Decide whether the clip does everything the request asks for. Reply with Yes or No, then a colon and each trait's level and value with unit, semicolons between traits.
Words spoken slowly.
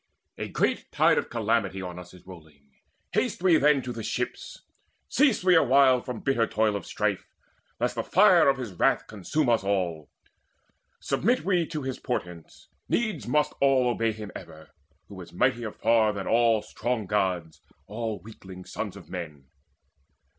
No: average, 165 wpm